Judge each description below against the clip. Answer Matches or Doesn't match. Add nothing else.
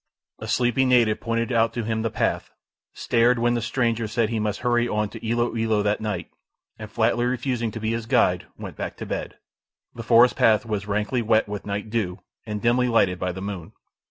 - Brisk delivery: Matches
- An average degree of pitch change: Doesn't match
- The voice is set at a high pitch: Doesn't match